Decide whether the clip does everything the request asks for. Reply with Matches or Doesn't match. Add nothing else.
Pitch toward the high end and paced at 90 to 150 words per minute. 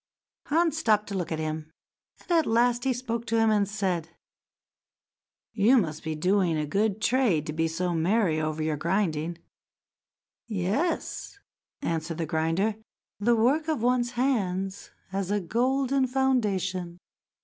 Matches